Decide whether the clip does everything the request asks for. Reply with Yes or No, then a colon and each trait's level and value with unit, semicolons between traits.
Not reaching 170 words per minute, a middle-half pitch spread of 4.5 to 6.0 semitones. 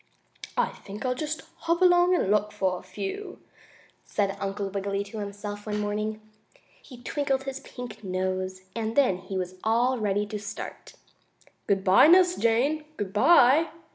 Yes: average, 160 wpm; average, 5.3 semitones